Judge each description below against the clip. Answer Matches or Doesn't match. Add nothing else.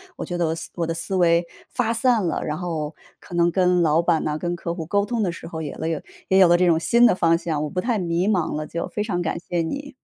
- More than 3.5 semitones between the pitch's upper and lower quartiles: Doesn't match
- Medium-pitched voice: Matches